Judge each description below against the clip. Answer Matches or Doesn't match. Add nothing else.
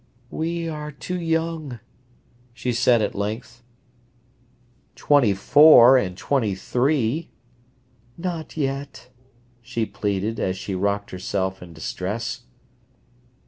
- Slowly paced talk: Matches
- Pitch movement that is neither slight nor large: Doesn't match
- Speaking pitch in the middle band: Doesn't match